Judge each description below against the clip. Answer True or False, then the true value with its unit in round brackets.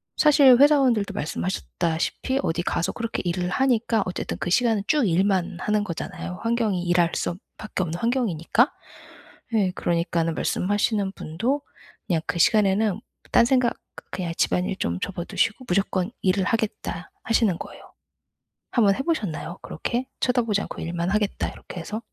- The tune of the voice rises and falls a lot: False (4.8 semitones)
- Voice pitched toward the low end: False (200 Hz)